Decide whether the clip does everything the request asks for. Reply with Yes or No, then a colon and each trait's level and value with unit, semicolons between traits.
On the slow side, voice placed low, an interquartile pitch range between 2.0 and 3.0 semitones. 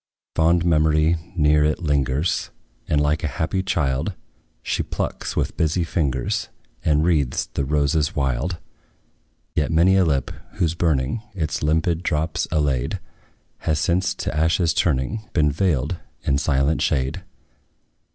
Yes: slow, 130 wpm; very low, 75 Hz; average, 2.7 semitones